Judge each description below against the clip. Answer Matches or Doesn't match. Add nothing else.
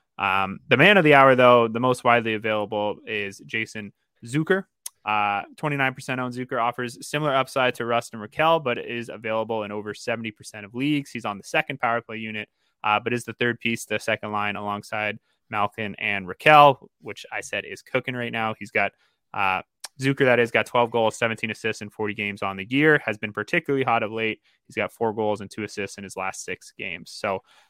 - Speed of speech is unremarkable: Doesn't match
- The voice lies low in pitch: Matches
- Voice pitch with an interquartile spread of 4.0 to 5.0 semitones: Doesn't match